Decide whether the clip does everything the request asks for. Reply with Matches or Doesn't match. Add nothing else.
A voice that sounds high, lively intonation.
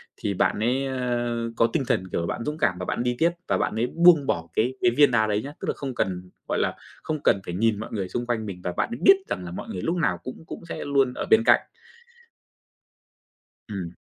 Doesn't match